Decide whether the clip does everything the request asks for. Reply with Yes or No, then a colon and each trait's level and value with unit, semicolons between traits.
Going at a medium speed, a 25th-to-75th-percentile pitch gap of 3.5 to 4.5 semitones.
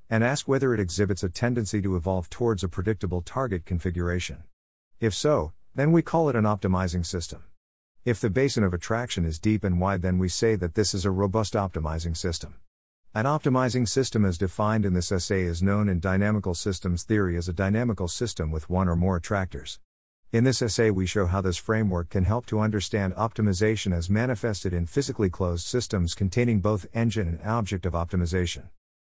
Yes: average, 190 wpm; average, 3.9 semitones